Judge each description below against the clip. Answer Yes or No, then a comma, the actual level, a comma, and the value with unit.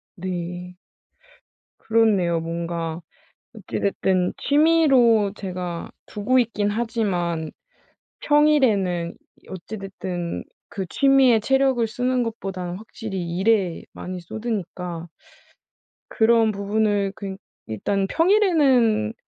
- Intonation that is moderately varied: Yes, average, 4.6 semitones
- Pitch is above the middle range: Yes, high, 200 Hz